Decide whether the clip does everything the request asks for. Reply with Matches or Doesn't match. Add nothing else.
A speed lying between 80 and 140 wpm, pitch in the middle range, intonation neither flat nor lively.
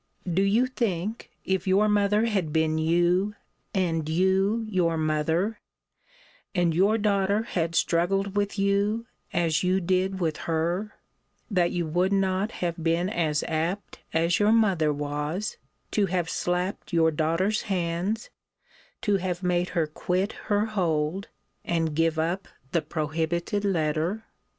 Matches